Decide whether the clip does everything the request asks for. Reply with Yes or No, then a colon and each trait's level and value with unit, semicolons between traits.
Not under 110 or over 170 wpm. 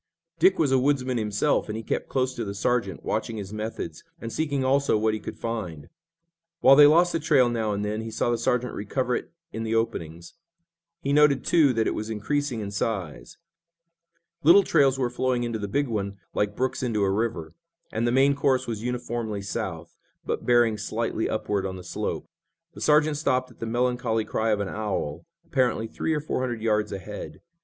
No: average, 200 wpm